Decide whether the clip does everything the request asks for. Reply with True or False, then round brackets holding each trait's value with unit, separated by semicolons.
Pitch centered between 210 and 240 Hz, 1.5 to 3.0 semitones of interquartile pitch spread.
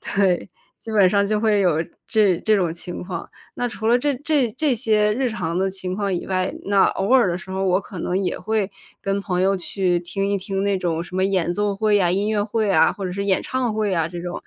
False (195 Hz; 2.7 semitones)